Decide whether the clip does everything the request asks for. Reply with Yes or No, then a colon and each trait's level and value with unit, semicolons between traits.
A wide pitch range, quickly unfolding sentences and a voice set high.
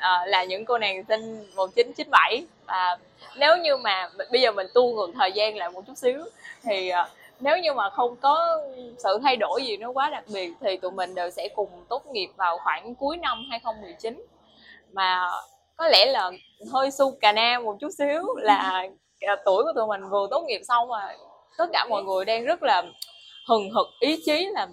No: wide, 6.8 semitones; average, 205 wpm; high, 235 Hz